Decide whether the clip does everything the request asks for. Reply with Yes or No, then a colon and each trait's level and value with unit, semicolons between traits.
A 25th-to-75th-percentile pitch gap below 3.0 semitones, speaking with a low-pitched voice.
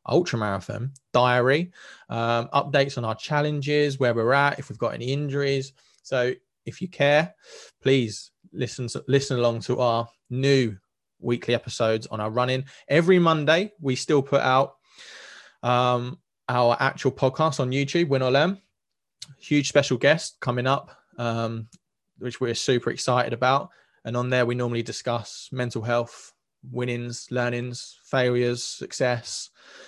Yes: narrow, 2.6 semitones; low, 125 Hz